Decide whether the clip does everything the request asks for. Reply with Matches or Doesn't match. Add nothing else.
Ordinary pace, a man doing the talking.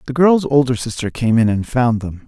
Doesn't match